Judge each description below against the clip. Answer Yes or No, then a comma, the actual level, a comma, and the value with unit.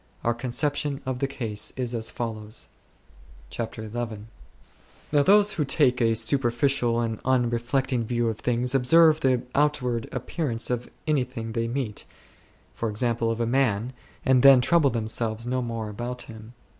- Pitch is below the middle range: Yes, low, 120 Hz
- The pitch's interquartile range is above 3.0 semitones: No, average, 2.7 semitones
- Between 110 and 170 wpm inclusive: Yes, average, 155 wpm